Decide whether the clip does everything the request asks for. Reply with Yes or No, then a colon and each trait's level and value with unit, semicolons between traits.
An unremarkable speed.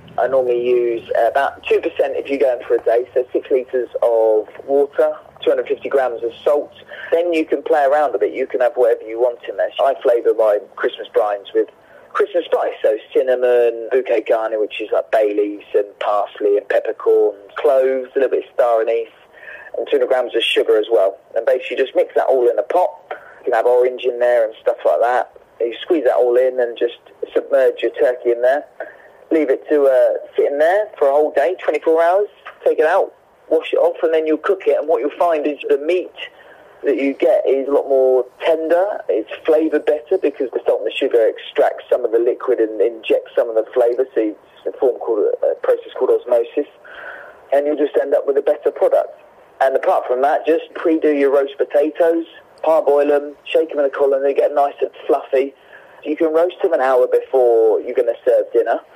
No: fast, 215 wpm